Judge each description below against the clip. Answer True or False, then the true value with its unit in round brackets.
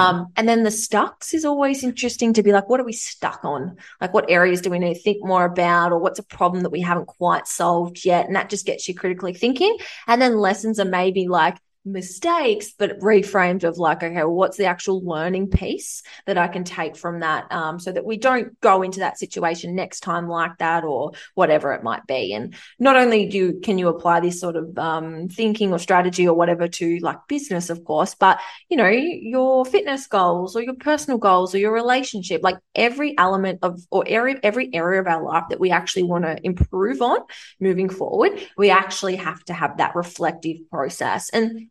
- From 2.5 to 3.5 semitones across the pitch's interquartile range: False (4.4 semitones)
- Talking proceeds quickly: True (215 wpm)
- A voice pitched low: False (185 Hz)